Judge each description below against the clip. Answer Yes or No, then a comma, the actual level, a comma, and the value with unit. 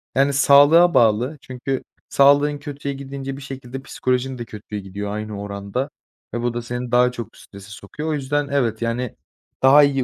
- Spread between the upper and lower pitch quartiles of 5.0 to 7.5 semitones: No, average, 3.3 semitones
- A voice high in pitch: No, low, 130 Hz